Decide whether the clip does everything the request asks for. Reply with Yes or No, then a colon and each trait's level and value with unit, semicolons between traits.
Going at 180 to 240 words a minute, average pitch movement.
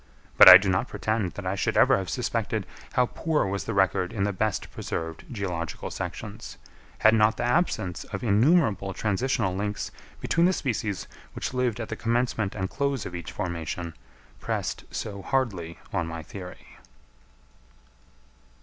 No: average, 160 wpm; average, 4.4 semitones